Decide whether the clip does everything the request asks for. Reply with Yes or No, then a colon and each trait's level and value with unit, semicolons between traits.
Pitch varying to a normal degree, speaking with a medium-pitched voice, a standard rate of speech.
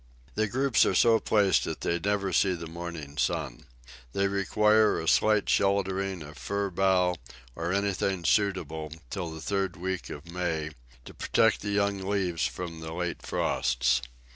No: average, 3.4 semitones; very low, 95 Hz; average, 160 wpm